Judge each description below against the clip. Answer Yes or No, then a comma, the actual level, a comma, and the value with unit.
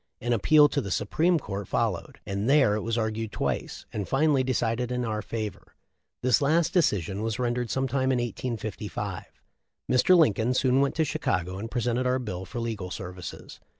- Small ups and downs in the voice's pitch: No, average, 4.0 semitones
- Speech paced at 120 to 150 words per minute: No, average, 180 wpm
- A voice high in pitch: No, low, 120 Hz